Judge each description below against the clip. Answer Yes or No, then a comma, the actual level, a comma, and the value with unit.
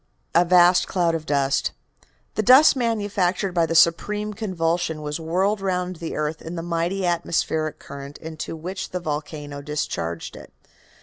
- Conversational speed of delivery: Yes, average, 150 wpm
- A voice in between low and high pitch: Yes, medium, 170 Hz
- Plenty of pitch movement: No, average, 3.1 semitones